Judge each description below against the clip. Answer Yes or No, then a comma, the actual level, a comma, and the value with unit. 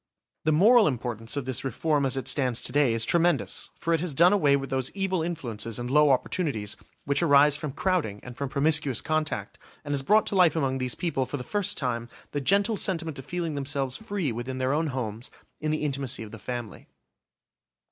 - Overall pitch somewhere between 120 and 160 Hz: Yes, medium, 140 Hz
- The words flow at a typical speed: No, fast, 210 wpm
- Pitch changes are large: No, average, 4.4 semitones